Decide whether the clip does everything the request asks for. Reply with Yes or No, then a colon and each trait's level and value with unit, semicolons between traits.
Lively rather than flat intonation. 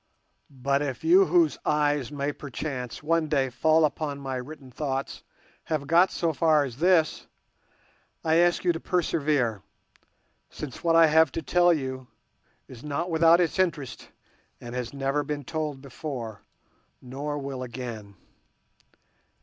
No: average, 3.5 semitones